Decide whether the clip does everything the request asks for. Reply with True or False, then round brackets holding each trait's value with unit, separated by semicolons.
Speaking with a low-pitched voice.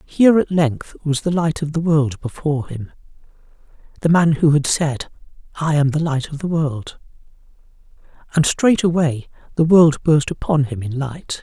False (150 Hz)